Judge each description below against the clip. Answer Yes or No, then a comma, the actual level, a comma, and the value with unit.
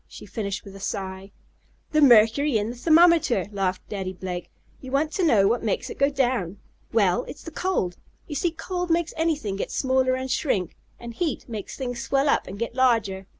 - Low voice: No, high, 240 Hz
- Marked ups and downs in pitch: Yes, wide, 6.7 semitones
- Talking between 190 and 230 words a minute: Yes, average, 195 wpm